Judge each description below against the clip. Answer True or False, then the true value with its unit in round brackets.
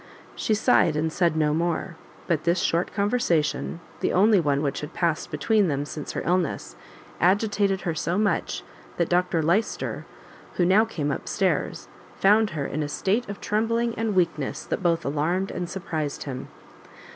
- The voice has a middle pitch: True (175 Hz)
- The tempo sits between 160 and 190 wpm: True (170 wpm)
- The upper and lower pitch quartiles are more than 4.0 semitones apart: True (4.6 semitones)